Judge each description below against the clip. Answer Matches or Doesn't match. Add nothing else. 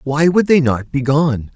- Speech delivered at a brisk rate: Matches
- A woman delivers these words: Doesn't match